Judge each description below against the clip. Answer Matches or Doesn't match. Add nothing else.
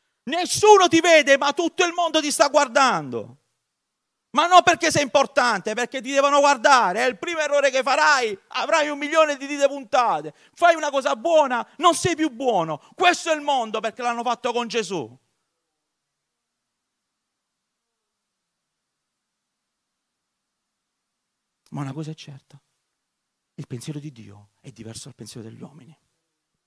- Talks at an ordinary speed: Matches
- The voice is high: Matches